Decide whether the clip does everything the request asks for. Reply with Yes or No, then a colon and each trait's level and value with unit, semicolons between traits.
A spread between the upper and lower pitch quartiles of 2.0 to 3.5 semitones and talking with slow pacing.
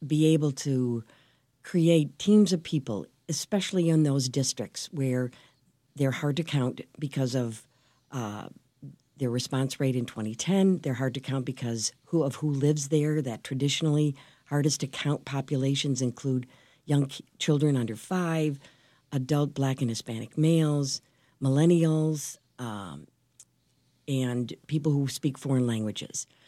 Yes: average, 3.1 semitones; slow, 130 wpm